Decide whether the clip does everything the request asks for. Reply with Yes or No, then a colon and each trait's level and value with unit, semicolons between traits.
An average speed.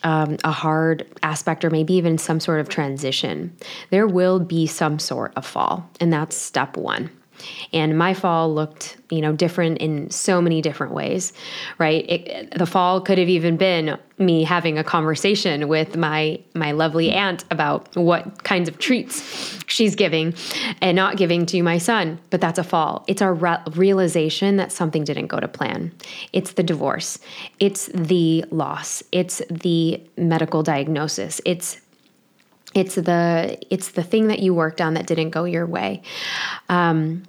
Yes: average, 165 wpm